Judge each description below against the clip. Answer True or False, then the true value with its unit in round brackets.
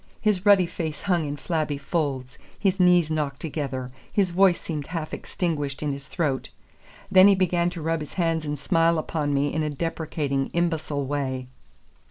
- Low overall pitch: False (155 Hz)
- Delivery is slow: False (175 wpm)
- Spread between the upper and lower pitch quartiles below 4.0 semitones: True (3.3 semitones)